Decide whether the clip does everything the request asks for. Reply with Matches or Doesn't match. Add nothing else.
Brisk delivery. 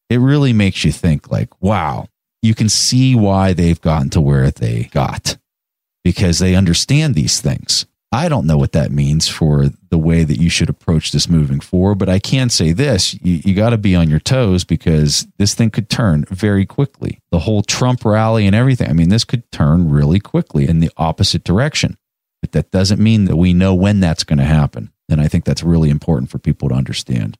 Matches